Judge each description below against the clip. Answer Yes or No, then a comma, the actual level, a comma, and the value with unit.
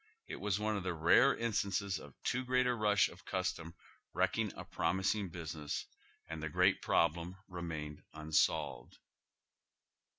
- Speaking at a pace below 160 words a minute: Yes, average, 140 wpm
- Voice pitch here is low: Yes, very low, 90 Hz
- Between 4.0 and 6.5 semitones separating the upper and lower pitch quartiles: Yes, average, 4.4 semitones